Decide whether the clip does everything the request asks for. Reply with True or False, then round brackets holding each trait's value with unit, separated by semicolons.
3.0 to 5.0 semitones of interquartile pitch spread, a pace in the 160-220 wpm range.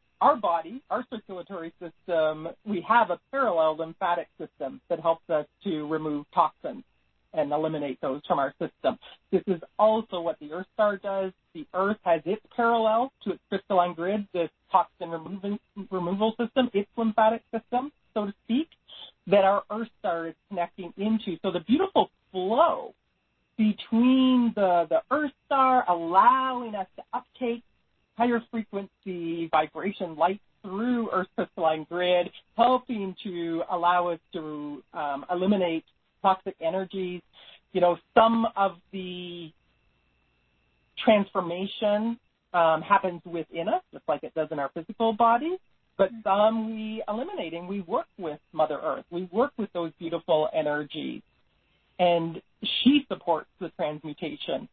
False (4.7 semitones; 140 wpm)